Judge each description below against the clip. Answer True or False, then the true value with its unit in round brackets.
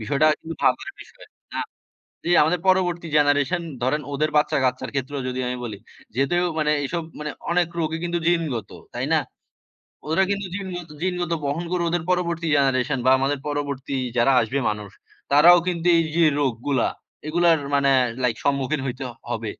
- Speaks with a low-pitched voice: False (150 Hz)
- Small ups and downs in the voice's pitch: False (4.3 semitones)